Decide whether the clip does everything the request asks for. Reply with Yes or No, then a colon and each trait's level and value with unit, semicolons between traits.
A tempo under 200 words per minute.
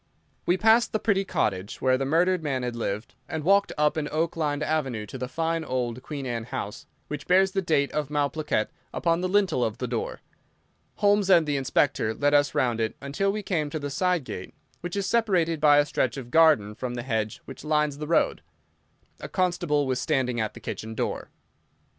No: fast, 205 wpm